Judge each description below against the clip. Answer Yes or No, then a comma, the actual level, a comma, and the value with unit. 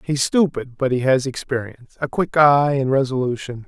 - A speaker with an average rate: Yes, average, 180 wpm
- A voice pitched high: No, low, 135 Hz